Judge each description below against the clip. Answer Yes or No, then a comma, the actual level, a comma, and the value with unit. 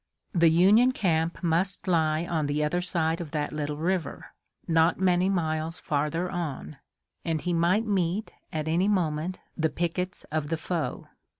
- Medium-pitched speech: Yes, medium, 165 Hz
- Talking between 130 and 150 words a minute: No, average, 160 wpm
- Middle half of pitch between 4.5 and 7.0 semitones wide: No, narrow, 2.4 semitones